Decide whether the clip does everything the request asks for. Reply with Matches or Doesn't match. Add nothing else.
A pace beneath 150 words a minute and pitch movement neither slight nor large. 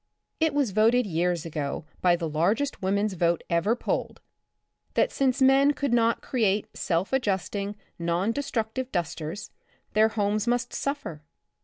Doesn't match